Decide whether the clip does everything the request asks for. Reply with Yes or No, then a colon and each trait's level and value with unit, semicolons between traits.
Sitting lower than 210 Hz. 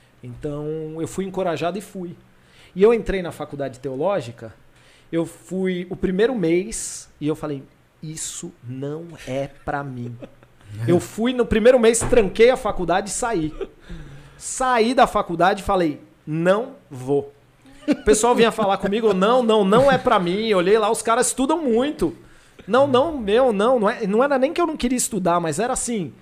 Yes: high, 190 Hz